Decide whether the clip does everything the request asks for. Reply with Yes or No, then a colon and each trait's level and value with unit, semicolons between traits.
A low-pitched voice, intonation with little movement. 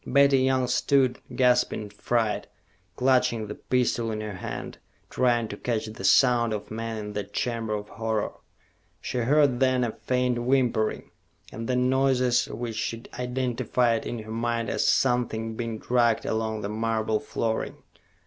Yes: low, 115 Hz; narrow, 2.3 semitones